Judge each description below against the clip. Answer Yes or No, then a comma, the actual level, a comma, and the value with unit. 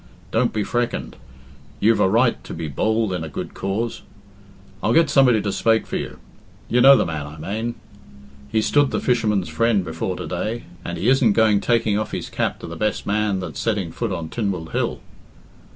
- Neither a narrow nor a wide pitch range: Yes, average, 3.9 semitones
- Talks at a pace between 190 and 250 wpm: Yes, average, 200 wpm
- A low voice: Yes, low, 105 Hz